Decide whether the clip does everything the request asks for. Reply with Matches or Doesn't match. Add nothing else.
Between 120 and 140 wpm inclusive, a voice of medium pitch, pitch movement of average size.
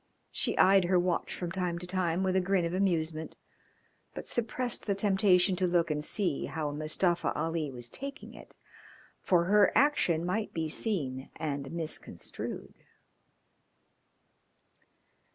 Matches